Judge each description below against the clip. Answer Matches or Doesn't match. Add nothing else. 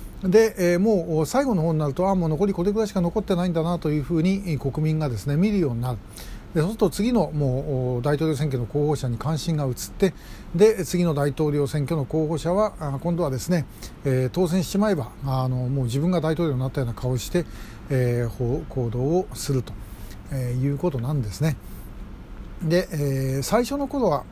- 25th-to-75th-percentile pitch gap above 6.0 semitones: Doesn't match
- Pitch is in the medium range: Matches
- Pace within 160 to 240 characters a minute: Doesn't match